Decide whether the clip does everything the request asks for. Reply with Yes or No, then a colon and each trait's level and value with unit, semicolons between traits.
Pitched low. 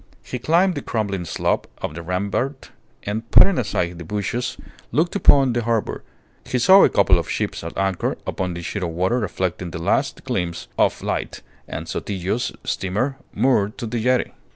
Yes: low, 105 Hz